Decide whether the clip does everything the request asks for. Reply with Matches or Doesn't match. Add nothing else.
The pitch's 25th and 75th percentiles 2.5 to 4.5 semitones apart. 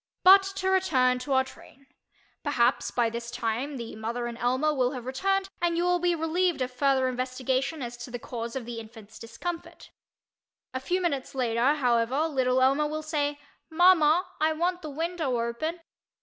Doesn't match